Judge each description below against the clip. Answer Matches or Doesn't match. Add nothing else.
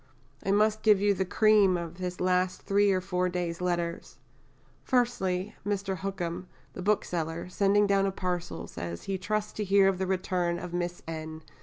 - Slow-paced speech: Doesn't match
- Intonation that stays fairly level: Matches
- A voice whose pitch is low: Doesn't match